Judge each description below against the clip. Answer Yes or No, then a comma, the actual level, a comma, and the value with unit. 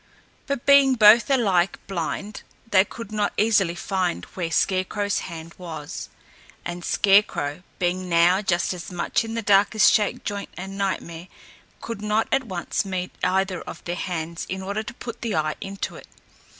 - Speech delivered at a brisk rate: No, average, 165 wpm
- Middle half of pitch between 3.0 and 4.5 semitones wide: Yes, average, 3.3 semitones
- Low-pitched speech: No, high, 195 Hz